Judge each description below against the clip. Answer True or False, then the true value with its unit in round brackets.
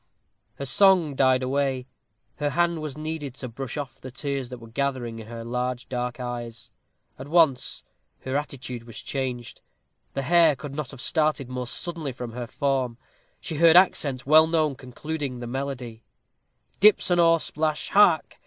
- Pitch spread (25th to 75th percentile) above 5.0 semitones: False (3.8 semitones)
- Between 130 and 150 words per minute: False (165 wpm)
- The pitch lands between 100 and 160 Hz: True (135 Hz)